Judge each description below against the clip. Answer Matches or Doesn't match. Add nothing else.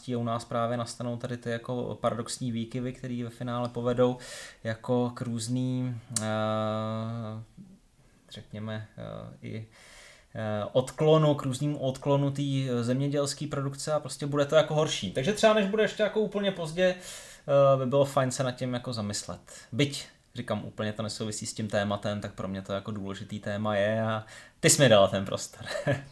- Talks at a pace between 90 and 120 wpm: Doesn't match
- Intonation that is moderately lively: Matches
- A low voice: Matches